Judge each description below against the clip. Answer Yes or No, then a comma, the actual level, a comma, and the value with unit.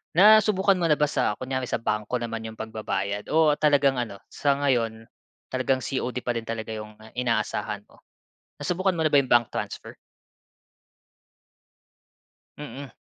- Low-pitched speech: Yes, low, 130 Hz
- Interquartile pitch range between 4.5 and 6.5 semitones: Yes, average, 5.1 semitones